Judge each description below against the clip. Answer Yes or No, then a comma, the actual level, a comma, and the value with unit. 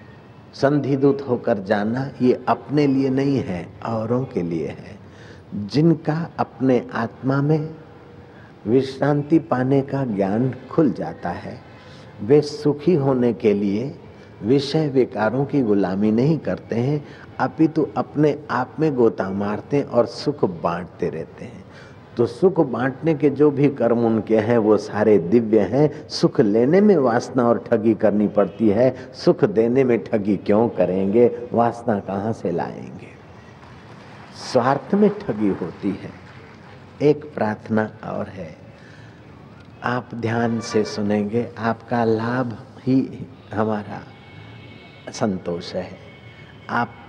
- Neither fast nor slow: Yes, average, 125 wpm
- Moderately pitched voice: No, low, 120 Hz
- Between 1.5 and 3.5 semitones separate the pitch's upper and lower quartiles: No, average, 4.3 semitones